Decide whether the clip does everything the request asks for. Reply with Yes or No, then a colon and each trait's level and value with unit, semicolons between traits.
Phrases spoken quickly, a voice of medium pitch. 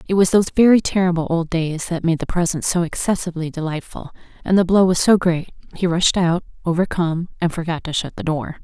Yes: fast, 210 wpm; medium, 170 Hz